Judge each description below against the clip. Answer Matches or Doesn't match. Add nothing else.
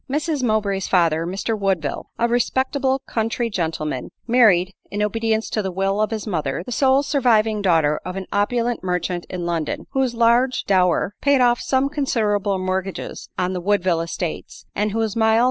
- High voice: Matches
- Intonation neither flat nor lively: Matches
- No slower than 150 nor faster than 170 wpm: Matches